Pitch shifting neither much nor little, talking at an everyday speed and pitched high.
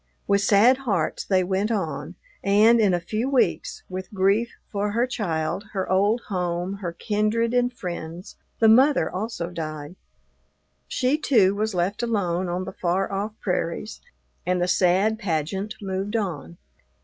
Yes: average, 3.6 semitones; average, 150 wpm; high, 195 Hz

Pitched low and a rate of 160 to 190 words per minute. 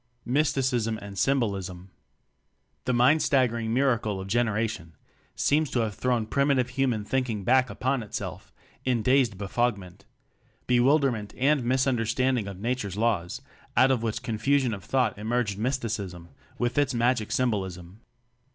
No: low, 120 Hz; slow, 135 wpm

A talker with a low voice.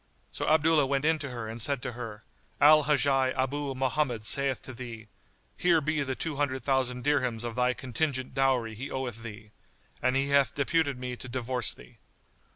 Yes: low, 130 Hz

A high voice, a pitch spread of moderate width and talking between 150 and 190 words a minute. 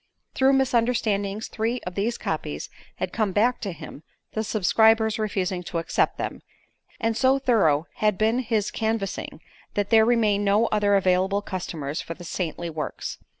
Yes: high, 210 Hz; average, 3.2 semitones; average, 155 wpm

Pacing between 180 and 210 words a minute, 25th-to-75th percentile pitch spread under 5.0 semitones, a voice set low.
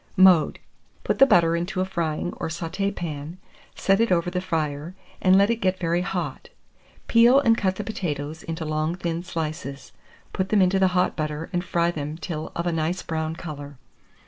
No: average, 190 wpm; average, 3.0 semitones; medium, 170 Hz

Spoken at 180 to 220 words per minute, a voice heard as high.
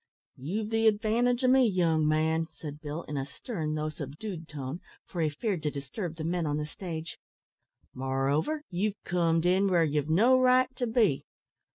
No: average, 185 wpm; medium, 165 Hz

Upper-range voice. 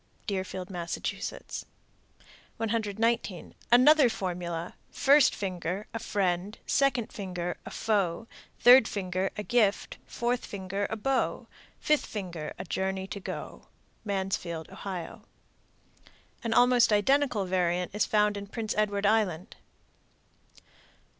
Yes: high, 200 Hz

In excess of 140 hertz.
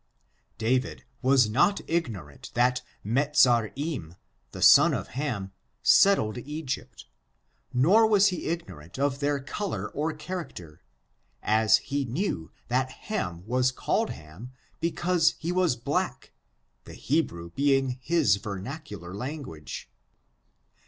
No: low, 130 Hz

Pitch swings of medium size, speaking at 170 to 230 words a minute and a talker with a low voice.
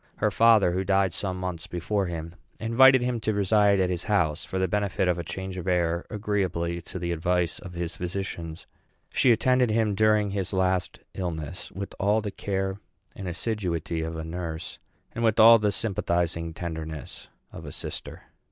Yes: average, 3.3 semitones; average, 180 wpm; very low, 95 Hz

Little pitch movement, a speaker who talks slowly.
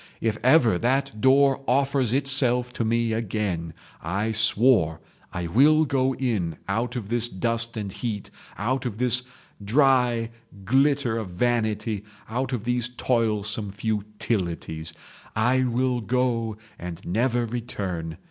No: average, 3.4 semitones; slow, 130 wpm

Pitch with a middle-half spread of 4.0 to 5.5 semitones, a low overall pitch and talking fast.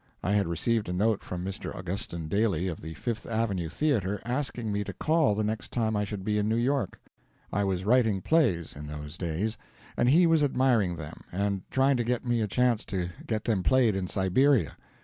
Yes: average, 4.6 semitones; low, 105 Hz; fast, 210 wpm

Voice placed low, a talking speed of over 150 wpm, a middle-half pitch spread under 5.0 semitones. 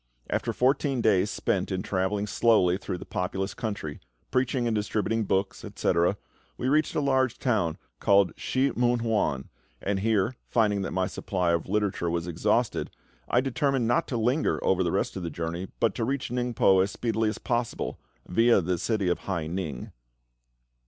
Yes: low, 105 Hz; average, 170 wpm; average, 4.6 semitones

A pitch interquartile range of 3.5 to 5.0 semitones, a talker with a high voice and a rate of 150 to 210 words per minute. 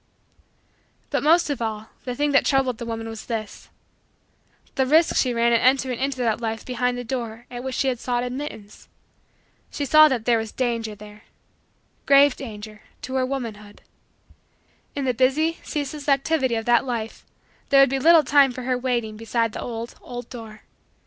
No: average, 3.1 semitones; high, 245 Hz; average, 180 wpm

